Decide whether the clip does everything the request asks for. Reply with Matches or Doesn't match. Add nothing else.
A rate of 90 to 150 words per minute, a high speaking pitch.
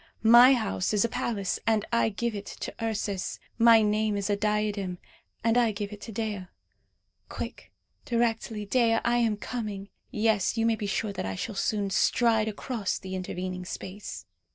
Doesn't match